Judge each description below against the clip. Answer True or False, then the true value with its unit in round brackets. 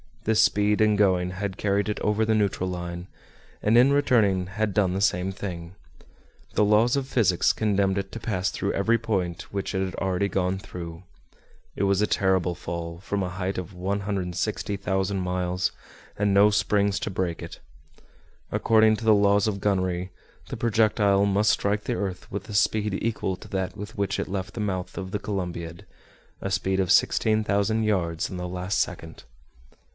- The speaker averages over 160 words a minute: True (180 wpm)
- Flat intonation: True (2.3 semitones)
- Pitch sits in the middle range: False (100 Hz)